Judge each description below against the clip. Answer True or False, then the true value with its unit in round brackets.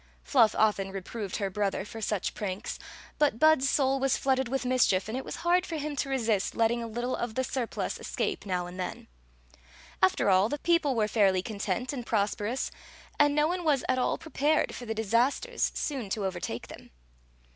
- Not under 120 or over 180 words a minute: False (205 wpm)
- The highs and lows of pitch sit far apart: False (5.0 semitones)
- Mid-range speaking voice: False (235 Hz)